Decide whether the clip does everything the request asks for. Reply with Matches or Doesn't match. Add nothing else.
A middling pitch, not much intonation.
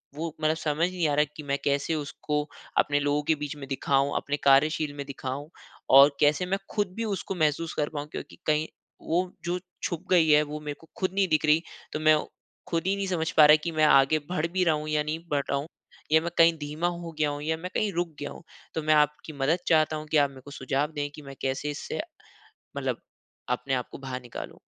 Matches